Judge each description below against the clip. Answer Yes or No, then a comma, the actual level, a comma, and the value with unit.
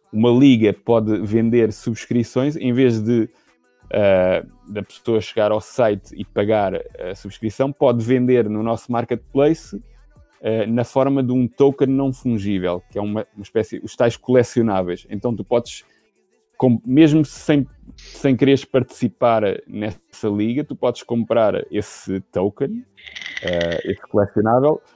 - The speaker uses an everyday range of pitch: Yes, average, 3.5 semitones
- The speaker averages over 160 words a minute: No, average, 140 wpm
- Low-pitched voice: Yes, low, 115 Hz